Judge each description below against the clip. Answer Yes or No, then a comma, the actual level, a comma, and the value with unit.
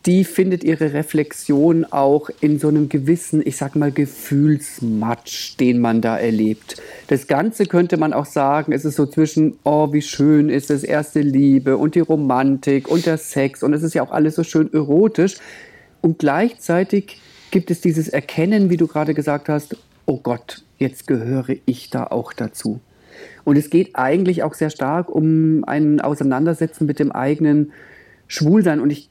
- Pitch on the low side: No, medium, 150 Hz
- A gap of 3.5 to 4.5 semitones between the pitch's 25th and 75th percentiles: No, narrow, 2.5 semitones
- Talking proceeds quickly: No, average, 175 wpm